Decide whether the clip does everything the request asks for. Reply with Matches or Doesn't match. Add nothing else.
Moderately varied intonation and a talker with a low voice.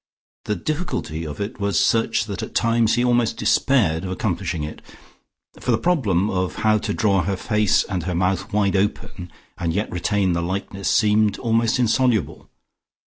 Matches